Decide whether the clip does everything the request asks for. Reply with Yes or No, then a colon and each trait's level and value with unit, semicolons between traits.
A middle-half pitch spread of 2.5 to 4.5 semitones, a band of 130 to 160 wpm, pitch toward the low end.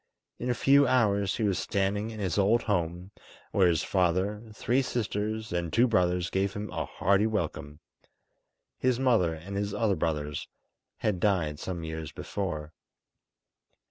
Yes: average, 4.0 semitones; average, 150 wpm; low, 100 Hz